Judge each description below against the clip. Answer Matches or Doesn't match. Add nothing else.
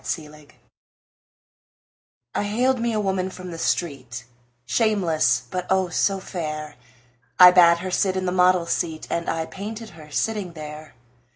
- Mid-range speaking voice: Matches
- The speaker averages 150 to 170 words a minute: Matches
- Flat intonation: Doesn't match